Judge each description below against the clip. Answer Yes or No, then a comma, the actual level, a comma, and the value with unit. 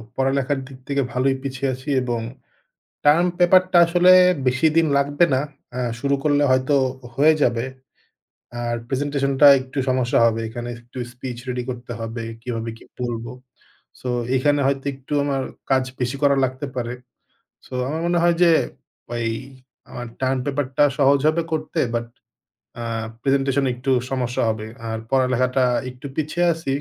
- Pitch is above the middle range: No, low, 135 Hz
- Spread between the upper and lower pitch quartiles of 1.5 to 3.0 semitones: Yes, narrow, 2.5 semitones